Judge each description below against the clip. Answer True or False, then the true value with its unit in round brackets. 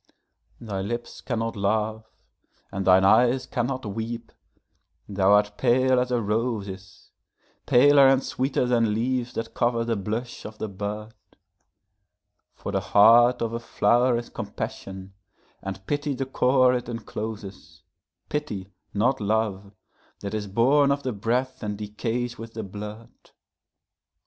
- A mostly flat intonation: False (3.3 semitones)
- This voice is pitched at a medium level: False (115 Hz)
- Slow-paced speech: True (130 wpm)